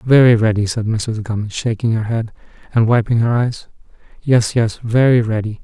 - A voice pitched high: No, low, 115 Hz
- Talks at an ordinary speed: Yes, average, 170 wpm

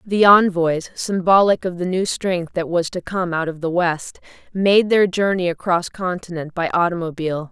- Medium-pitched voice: Yes, medium, 180 Hz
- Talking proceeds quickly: No, average, 175 wpm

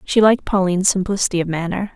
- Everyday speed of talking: Yes, average, 185 wpm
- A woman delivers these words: Yes, female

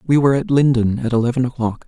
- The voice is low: Yes, low, 130 Hz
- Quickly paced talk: Yes, fast, 225 wpm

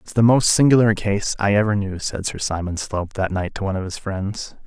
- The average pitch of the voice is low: Yes, low, 100 Hz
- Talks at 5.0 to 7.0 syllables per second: Yes, 5.5 syllables/s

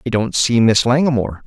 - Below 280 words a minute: Yes, fast, 205 wpm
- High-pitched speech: No, low, 120 Hz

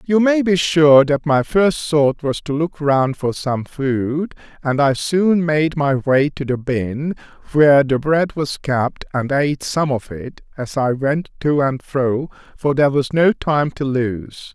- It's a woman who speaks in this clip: No, male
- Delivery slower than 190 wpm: No, average, 195 wpm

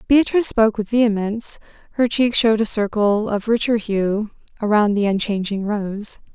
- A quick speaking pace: No, average, 150 wpm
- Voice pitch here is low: No, high, 215 Hz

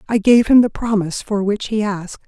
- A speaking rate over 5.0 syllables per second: Yes, 5.7 syllables/s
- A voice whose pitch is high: Yes, high, 210 Hz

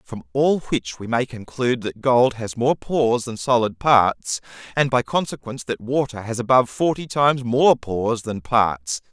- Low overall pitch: Yes, low, 120 Hz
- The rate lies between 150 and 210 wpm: Yes, average, 180 wpm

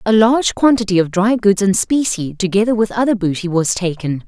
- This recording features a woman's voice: Yes, female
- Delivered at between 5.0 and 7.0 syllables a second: Yes, 5.6 syllables/s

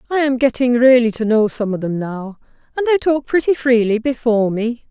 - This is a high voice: Yes, high, 245 Hz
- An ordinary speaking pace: No, fast, 210 wpm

